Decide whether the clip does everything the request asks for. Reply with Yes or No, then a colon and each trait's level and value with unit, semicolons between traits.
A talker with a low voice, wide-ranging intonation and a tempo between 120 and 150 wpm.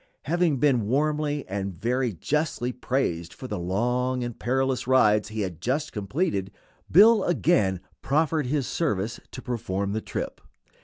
Yes: low, 125 Hz; wide, 6.0 semitones; average, 145 wpm